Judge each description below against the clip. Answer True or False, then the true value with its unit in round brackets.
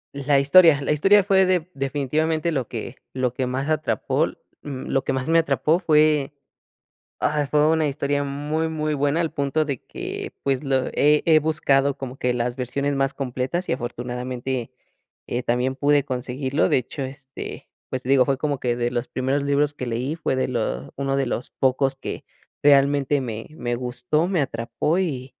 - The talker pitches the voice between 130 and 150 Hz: True (140 Hz)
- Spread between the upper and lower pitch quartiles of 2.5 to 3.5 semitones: True (2.9 semitones)